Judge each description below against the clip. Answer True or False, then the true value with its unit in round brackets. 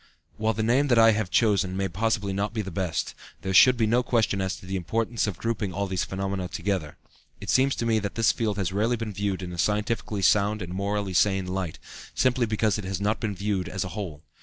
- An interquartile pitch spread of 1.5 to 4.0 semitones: True (2.8 semitones)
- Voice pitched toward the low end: True (100 Hz)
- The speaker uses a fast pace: True (235 wpm)